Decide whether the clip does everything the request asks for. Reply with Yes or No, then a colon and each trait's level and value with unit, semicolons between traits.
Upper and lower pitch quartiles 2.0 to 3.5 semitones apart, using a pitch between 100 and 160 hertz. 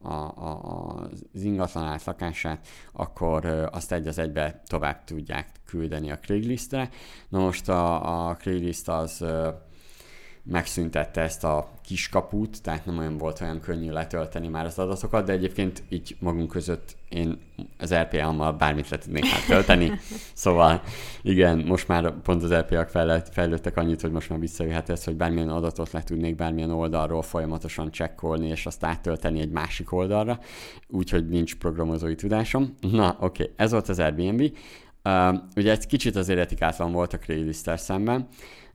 No: narrow, 2.4 semitones; very low, 85 Hz